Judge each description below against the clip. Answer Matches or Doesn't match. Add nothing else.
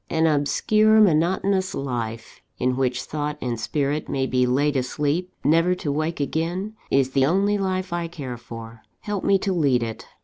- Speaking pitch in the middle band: Matches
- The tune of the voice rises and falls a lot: Matches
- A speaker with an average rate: Matches